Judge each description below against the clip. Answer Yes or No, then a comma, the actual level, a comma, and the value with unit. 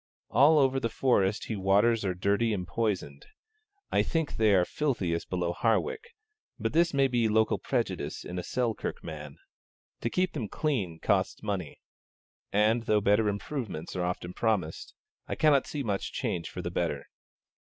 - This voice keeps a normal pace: Yes, average, 165 wpm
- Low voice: Yes, low, 110 Hz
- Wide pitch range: Yes, wide, 5.7 semitones